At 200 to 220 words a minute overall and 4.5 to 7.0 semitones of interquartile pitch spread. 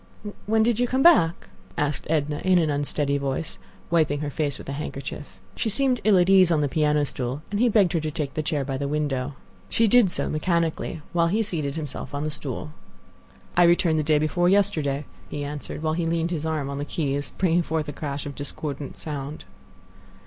No: fast, 205 wpm; average, 3.3 semitones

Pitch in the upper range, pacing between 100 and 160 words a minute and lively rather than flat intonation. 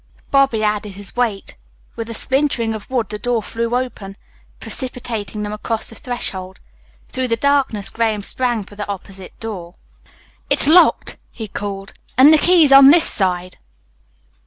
No: high, 225 Hz; average, 155 wpm; average, 4.0 semitones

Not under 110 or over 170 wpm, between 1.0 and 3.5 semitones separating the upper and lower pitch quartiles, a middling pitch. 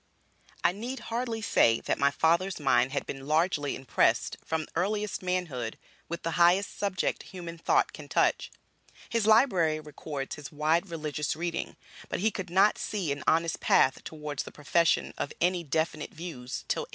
No: average, 165 wpm; average, 3.9 semitones; medium, 165 Hz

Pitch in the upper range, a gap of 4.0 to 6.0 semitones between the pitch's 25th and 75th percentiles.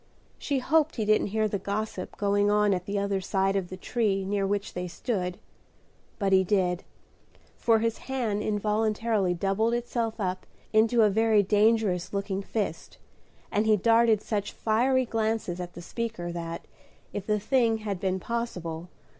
No: high, 205 Hz; average, 2.7 semitones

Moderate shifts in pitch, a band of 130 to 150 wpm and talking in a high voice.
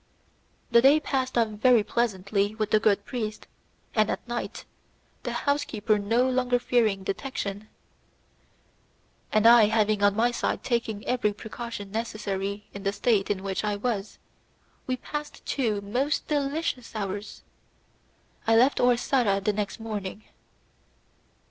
Yes: average, 3.3 semitones; slow, 135 wpm; high, 220 Hz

